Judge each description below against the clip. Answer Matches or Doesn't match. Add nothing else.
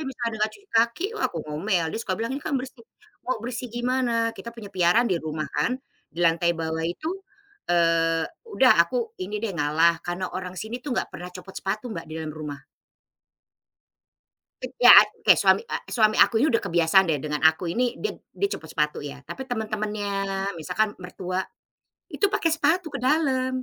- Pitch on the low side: Doesn't match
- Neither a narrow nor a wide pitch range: Doesn't match